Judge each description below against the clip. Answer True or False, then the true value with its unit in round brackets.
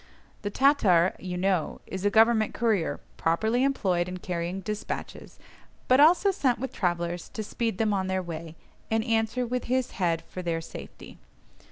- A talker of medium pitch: False (205 Hz)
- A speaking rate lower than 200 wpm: True (165 wpm)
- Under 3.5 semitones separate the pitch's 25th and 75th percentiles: False (5.0 semitones)